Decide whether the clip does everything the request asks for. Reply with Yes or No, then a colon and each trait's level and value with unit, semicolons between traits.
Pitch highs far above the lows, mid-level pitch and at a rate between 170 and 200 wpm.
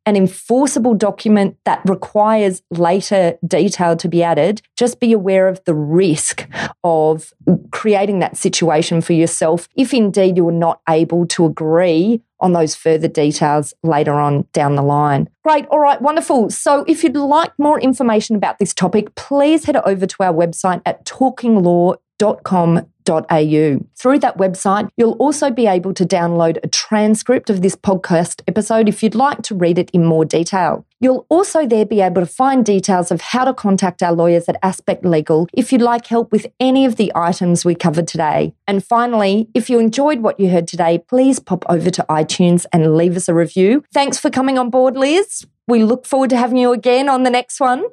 No: wide, 6.3 semitones; high, 195 Hz; average, 190 wpm